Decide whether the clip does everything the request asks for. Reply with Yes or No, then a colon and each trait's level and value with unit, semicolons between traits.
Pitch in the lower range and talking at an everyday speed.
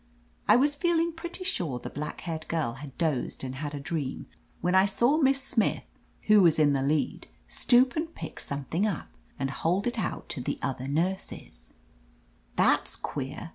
No: medium, 165 Hz; average, 180 wpm